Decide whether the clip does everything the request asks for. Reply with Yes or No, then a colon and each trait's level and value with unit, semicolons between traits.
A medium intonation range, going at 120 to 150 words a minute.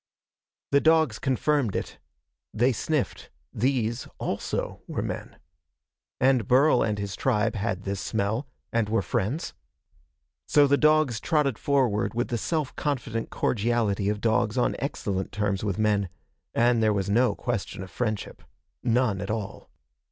Yes: average, 4.3 semitones; average, 145 wpm